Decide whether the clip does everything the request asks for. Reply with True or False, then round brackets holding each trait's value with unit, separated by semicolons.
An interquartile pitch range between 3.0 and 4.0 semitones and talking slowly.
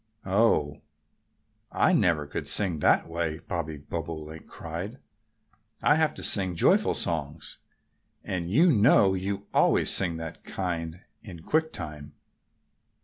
True (3.7 semitones; 125 wpm)